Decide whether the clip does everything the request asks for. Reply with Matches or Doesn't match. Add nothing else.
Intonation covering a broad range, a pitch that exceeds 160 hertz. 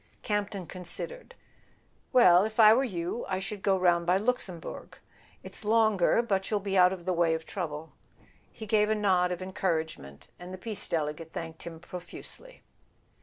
Doesn't match